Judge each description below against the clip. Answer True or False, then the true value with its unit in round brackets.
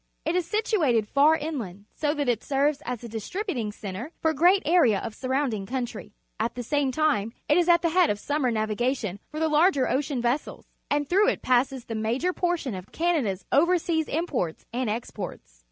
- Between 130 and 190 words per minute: False (205 wpm)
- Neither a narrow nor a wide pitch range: False (6.1 semitones)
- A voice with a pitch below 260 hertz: False (270 Hz)